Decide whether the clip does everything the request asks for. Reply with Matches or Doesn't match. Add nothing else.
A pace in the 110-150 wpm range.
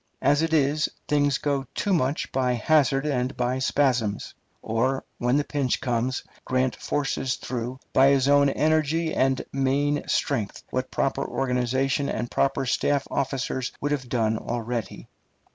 Matches